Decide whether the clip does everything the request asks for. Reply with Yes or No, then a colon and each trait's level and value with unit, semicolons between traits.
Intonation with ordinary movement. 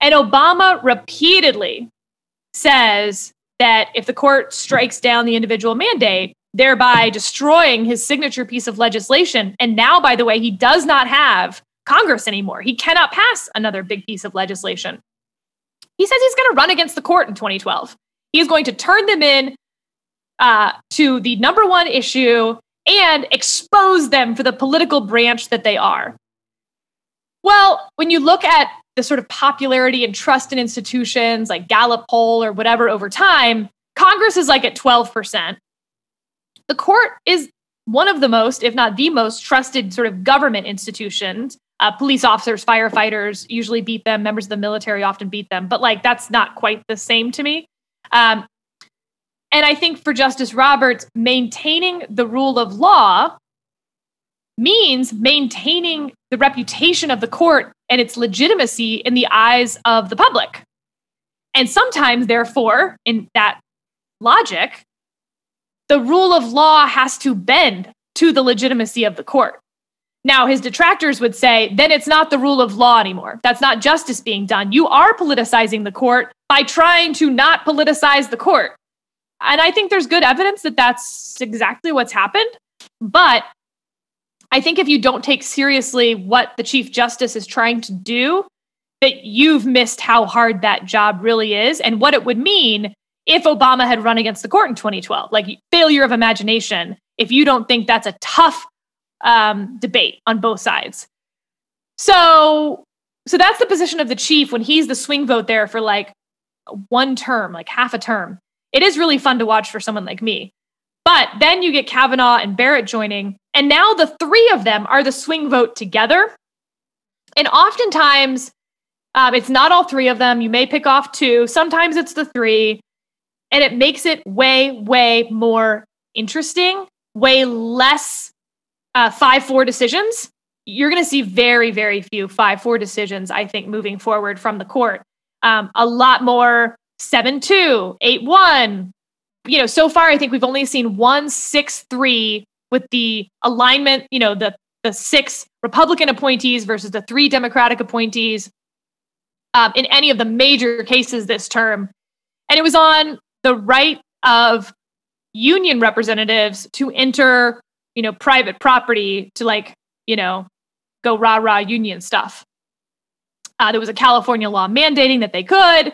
Yes: average, 4.3 semitones